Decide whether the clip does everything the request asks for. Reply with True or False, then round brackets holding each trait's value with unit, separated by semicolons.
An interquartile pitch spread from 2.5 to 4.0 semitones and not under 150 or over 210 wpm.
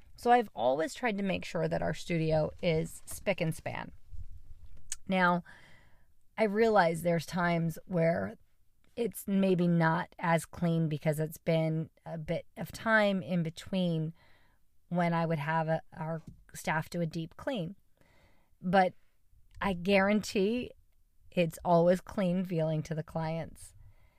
False (2.8 semitones; 135 wpm)